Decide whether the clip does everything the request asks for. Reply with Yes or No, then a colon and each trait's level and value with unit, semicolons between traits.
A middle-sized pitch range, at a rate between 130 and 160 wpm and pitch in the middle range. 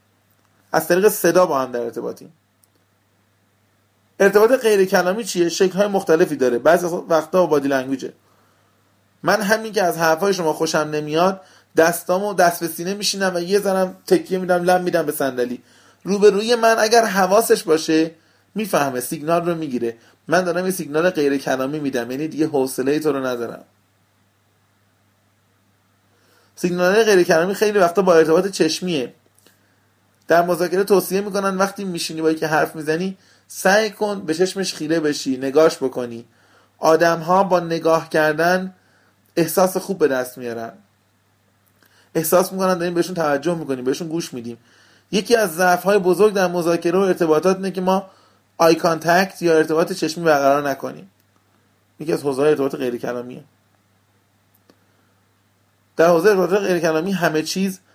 No: wide, 7.9 semitones; average, 145 wpm; medium, 160 Hz